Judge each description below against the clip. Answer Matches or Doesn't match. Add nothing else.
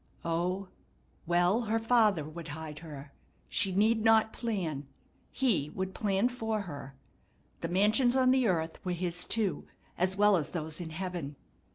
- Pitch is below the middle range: Doesn't match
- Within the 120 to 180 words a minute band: Matches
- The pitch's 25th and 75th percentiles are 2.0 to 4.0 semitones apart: Doesn't match